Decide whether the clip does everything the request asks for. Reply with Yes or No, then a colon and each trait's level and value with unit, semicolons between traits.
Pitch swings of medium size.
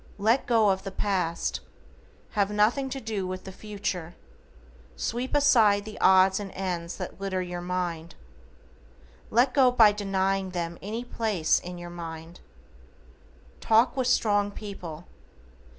Yes: average, 3.5 semitones